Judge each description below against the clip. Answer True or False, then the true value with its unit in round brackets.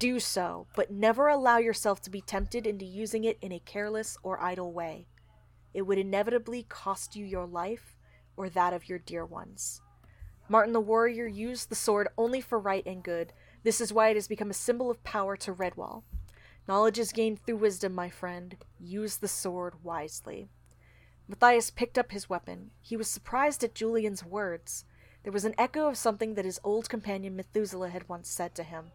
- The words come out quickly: False (190 wpm)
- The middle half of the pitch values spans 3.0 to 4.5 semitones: True (3.9 semitones)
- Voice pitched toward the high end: True (205 Hz)